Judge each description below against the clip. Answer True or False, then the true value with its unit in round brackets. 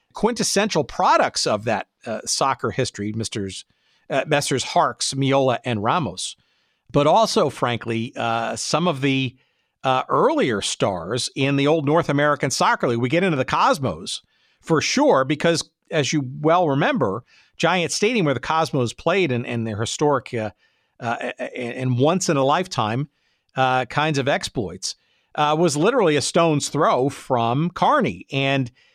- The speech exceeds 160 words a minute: False (150 wpm)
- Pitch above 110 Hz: True (140 Hz)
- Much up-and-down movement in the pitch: False (4.6 semitones)